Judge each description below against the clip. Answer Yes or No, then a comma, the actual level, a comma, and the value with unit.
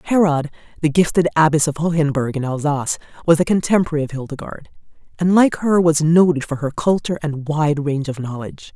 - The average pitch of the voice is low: No, medium, 155 Hz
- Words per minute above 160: Yes, average, 180 wpm